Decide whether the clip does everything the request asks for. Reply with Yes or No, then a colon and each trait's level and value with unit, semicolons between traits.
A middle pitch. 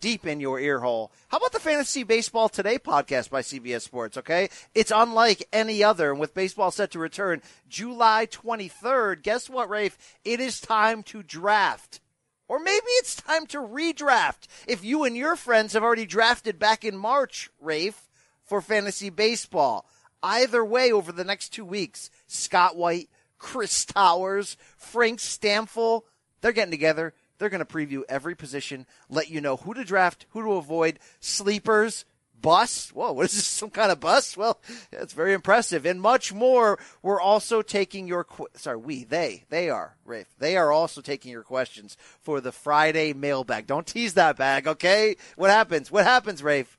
No: high, 205 Hz